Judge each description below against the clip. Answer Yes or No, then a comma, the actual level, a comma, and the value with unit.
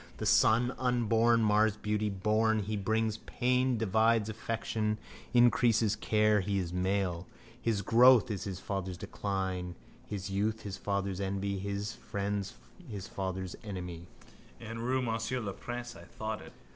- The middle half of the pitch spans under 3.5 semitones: Yes, narrow, 2.5 semitones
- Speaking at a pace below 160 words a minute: Yes, average, 150 wpm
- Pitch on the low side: Yes, low, 105 Hz